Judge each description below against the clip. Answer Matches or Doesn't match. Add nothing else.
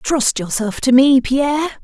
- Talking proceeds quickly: Doesn't match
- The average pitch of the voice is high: Matches